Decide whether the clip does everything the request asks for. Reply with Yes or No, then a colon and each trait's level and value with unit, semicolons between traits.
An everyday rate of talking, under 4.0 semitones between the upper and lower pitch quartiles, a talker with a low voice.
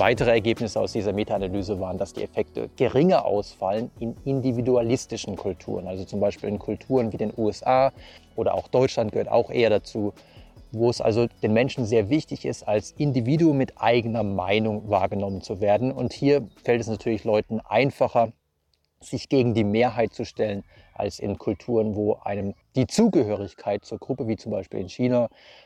Yes: average, 170 wpm; average, 3.3 semitones; low, 110 Hz